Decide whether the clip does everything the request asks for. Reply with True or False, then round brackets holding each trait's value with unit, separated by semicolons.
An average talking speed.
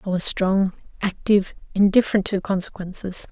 False (125 wpm)